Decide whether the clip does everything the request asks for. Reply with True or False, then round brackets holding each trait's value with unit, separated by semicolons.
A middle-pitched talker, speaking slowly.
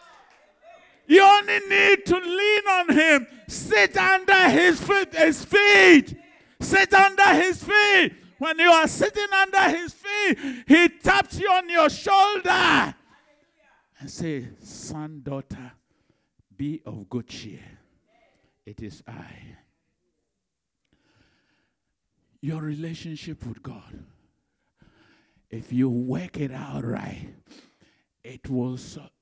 False (320 Hz; 110 wpm)